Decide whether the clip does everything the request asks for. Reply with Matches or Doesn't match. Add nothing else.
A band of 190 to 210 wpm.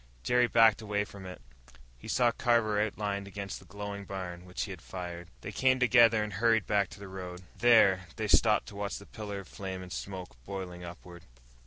Matches